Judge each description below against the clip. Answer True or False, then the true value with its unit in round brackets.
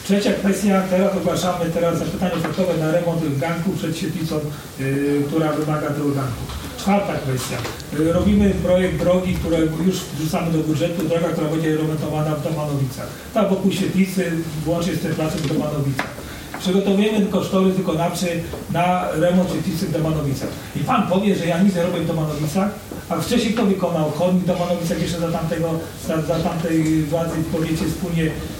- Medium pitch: True (170 Hz)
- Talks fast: True (165 wpm)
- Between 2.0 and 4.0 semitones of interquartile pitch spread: True (2.4 semitones)